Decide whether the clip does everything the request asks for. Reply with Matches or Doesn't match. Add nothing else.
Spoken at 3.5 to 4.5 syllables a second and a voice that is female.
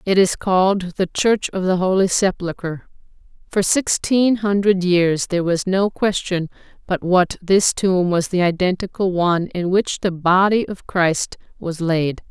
Matches